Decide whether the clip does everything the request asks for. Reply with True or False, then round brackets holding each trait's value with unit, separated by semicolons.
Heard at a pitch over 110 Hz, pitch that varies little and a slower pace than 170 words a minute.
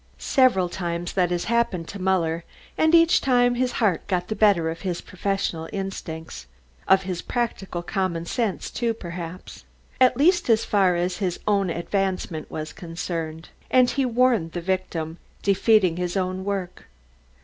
False (185 Hz; 4.1 semitones; 155 wpm)